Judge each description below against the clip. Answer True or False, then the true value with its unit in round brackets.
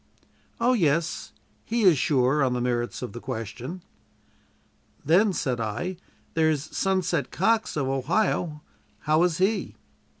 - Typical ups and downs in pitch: False (6.3 semitones)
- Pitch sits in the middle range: True (155 Hz)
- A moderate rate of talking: False (130 wpm)